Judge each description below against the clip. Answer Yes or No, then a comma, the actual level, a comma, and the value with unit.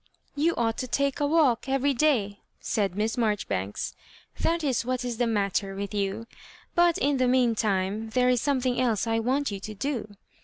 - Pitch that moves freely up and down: No, average, 4.5 semitones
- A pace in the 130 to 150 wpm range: No, fast, 205 wpm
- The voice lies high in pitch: Yes, high, 235 Hz